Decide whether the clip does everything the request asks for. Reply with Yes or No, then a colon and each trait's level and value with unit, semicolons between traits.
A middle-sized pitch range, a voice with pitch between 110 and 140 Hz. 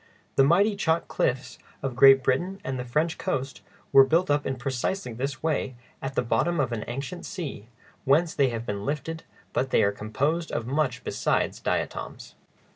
Yes: average, 4.3 semitones; low, 135 Hz